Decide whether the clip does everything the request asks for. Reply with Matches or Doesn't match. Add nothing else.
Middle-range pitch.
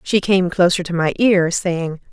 Matches